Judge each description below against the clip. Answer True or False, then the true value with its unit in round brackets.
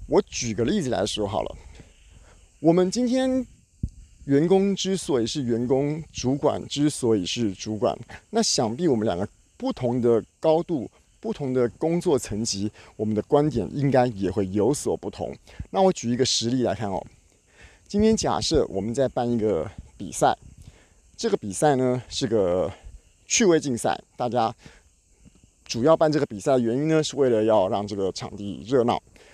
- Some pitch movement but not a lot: False (6.3 semitones)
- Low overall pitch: True (125 Hz)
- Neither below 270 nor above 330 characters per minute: False (240 characters per minute)